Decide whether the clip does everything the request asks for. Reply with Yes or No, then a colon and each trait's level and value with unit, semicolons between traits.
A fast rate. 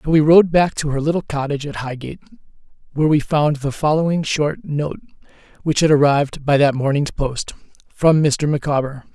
No: average, 175 wpm